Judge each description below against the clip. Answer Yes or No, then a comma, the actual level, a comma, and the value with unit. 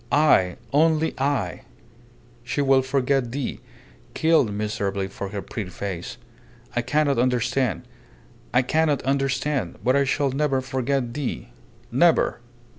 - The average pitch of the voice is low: Yes, low, 130 Hz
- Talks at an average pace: No, slow, 120 wpm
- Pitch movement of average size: Yes, average, 3.3 semitones